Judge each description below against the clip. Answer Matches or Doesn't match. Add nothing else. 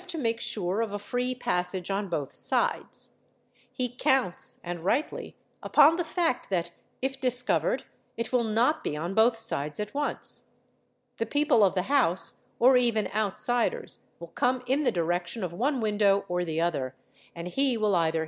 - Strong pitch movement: Matches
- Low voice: Doesn't match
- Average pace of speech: Matches